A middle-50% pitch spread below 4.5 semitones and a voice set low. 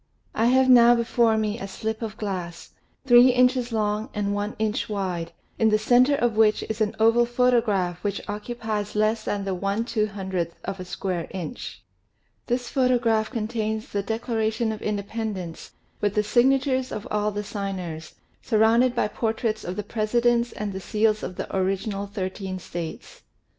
No: average, 2.9 semitones; high, 215 Hz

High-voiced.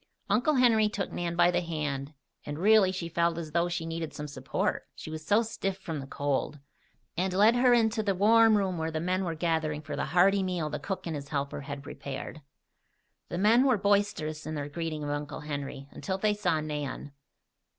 No: medium, 170 Hz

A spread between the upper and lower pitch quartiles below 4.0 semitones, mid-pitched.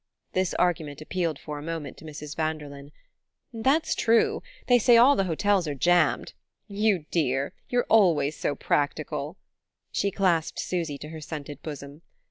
No: average, 4.8 semitones; medium, 160 Hz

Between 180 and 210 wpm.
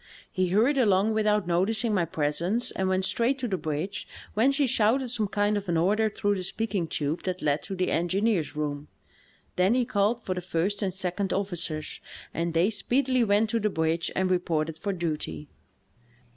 Yes: average, 185 wpm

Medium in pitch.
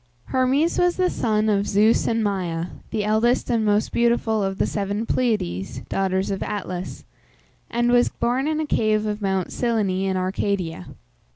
No: high, 215 Hz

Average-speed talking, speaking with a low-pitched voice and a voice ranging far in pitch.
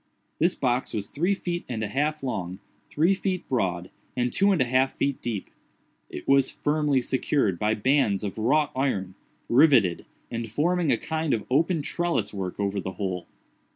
Yes: average, 170 wpm; low, 130 Hz; wide, 7.0 semitones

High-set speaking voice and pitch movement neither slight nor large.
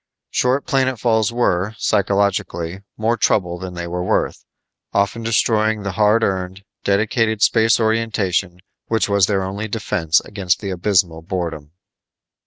No: low, 100 Hz; average, 3.4 semitones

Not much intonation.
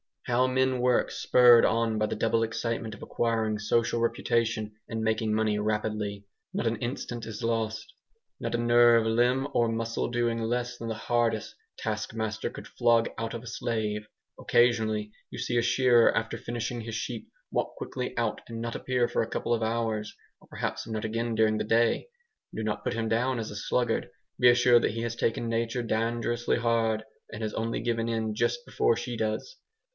Yes: narrow, 1.3 semitones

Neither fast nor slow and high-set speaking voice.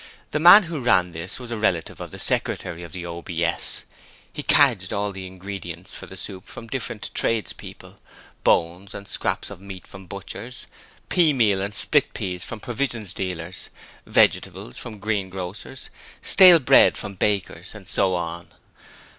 No: average, 155 wpm; very low, 95 Hz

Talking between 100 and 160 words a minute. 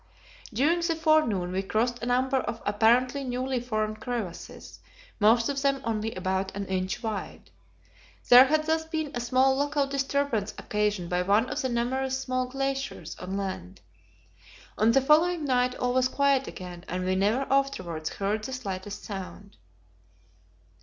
Yes: average, 155 wpm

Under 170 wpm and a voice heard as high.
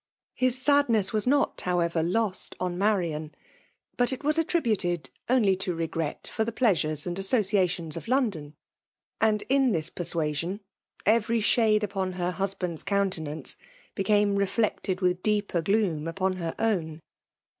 Yes: average, 140 wpm; high, 195 Hz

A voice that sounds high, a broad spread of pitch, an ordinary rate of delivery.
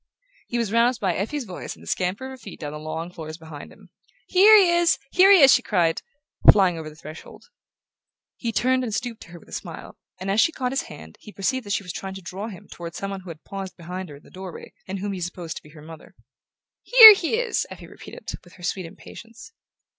No: high, 195 Hz; wide, 6.9 semitones; fast, 245 wpm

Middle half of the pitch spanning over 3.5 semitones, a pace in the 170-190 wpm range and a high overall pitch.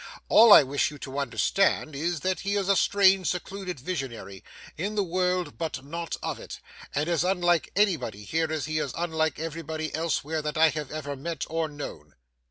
No: average, 3.9 semitones; average, 185 wpm; medium, 160 Hz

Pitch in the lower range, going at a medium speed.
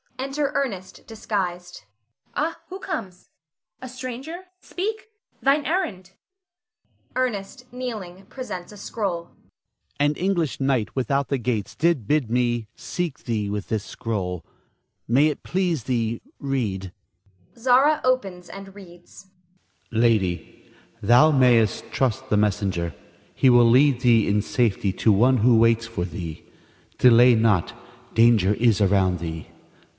No: low, 130 Hz; slow, 125 wpm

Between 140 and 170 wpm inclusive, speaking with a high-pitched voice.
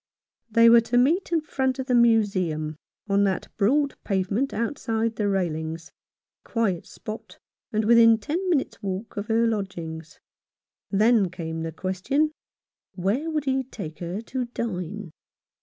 Yes: average, 155 wpm; high, 220 Hz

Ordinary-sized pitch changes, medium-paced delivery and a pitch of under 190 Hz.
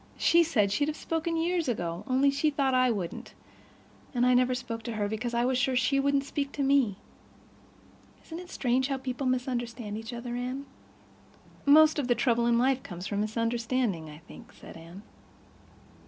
No: average, 3.3 semitones; average, 185 wpm; very high, 250 Hz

